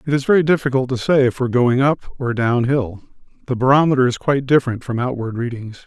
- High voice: No, low, 130 Hz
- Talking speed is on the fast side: Yes, fast, 225 wpm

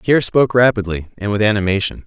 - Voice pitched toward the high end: No, low, 110 Hz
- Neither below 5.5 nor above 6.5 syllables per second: No, 6.9 syllables/s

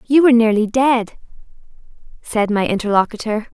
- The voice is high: Yes, high, 230 Hz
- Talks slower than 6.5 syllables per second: Yes, 5.4 syllables/s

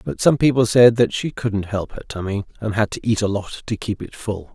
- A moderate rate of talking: No, fast, 265 wpm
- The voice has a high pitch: No, low, 110 Hz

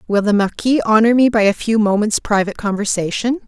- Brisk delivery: No, average, 190 wpm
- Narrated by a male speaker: No, female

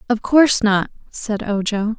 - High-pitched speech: Yes, high, 220 Hz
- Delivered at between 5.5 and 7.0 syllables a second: No, 4.3 syllables/s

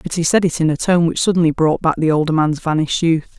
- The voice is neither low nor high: Yes, medium, 165 Hz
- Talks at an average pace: No, fast, 285 wpm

